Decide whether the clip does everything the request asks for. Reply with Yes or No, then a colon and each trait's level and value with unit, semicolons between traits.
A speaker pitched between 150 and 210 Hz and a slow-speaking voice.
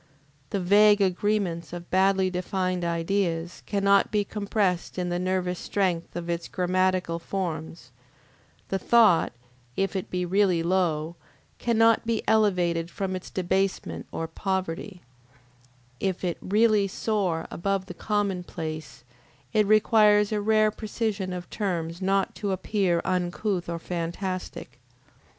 Yes: medium, 185 Hz; slow, 125 wpm